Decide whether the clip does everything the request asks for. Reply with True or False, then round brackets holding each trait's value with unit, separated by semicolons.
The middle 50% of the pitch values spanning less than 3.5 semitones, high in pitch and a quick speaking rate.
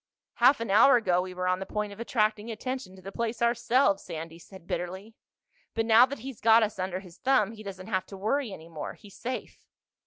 False (3.8 semitones; 210 Hz; 220 wpm)